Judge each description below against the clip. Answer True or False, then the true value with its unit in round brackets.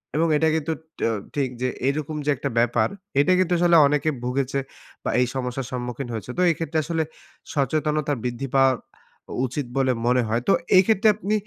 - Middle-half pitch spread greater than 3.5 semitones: True (4.2 semitones)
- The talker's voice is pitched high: False (140 Hz)